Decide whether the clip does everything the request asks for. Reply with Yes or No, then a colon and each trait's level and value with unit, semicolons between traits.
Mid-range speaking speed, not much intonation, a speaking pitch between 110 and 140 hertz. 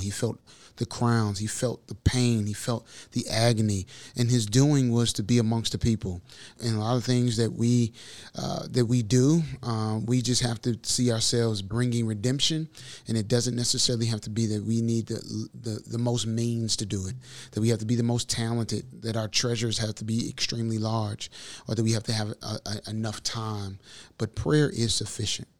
No: fast, 210 wpm; narrow, 1.9 semitones; low, 115 Hz